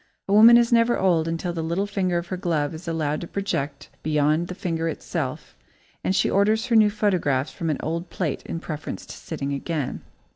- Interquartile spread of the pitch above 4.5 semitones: No, average, 4.2 semitones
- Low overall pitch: No, medium, 170 Hz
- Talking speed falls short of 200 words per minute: No, fast, 205 wpm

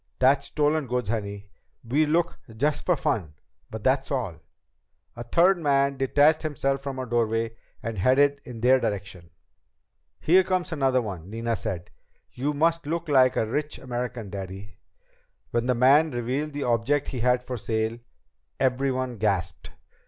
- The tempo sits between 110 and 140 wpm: No, average, 150 wpm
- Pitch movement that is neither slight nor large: Yes, average, 4.3 semitones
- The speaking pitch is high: No, low, 130 Hz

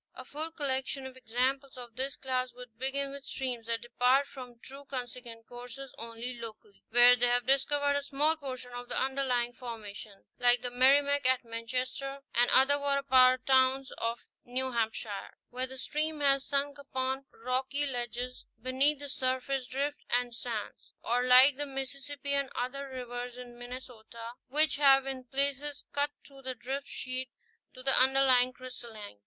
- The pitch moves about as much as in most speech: No, narrow, 2.0 semitones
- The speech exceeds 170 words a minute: No, average, 165 wpm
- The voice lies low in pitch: No, very high, 255 Hz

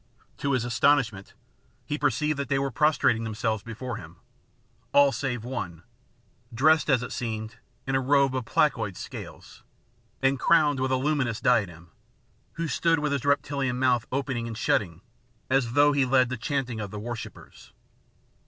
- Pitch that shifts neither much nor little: Yes, average, 3.7 semitones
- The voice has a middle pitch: No, low, 130 Hz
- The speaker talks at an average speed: Yes, average, 160 wpm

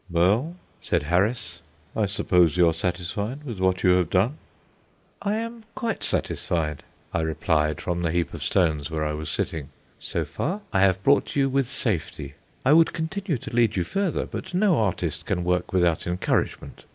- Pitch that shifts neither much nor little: No, wide, 8.3 semitones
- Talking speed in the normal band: Yes, average, 175 wpm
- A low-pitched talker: Yes, very low, 95 Hz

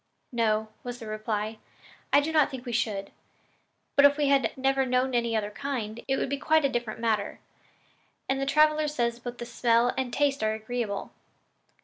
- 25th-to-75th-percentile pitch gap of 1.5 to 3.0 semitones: No, average, 3.7 semitones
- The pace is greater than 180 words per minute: Yes, average, 190 wpm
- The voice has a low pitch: No, high, 245 Hz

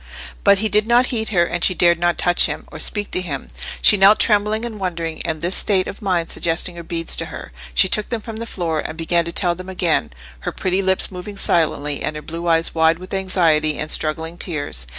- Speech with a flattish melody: No, average, 3.4 semitones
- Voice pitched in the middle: Yes, medium, 175 Hz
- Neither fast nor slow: No, fast, 230 wpm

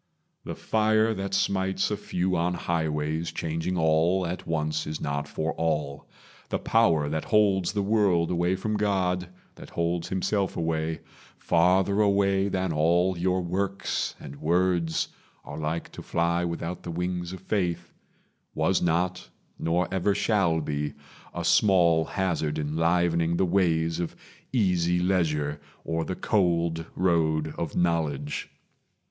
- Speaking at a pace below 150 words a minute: Yes, average, 140 wpm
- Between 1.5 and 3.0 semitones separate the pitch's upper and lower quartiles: Yes, narrow, 2.6 semitones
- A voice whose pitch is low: Yes, very low, 85 Hz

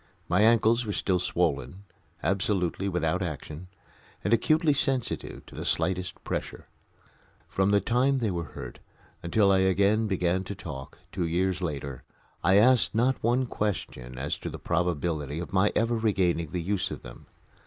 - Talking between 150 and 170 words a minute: Yes, average, 160 wpm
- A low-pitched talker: Yes, very low, 95 Hz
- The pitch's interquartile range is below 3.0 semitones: No, average, 4.0 semitones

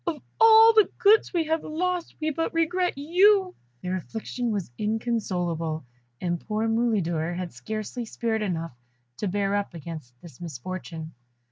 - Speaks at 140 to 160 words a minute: Yes, average, 145 wpm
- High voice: Yes, high, 215 Hz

